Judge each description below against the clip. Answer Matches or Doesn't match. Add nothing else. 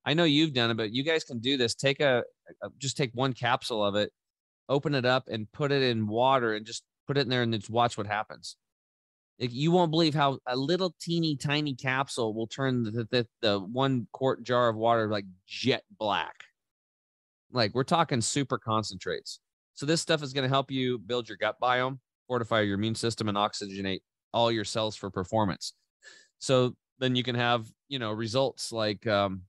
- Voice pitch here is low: Matches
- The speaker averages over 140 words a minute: Matches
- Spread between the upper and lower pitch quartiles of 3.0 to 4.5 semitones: Matches